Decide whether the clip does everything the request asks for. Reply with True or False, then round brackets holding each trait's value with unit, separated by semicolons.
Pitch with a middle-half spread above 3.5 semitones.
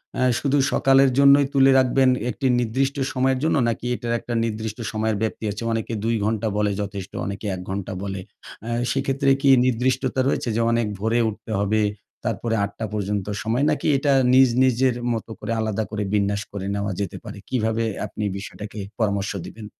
True (4.0 semitones)